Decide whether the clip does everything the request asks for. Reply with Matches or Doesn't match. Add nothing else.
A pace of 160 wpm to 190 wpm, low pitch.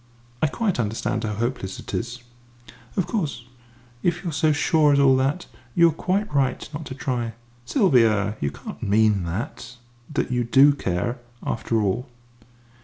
Matches